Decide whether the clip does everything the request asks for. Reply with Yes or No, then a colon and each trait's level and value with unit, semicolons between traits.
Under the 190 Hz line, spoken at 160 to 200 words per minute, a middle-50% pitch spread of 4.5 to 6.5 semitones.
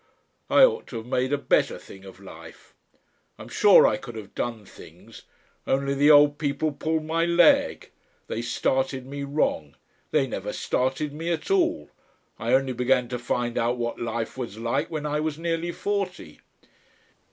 Yes: low, 135 Hz; average, 170 wpm; average, 4.8 semitones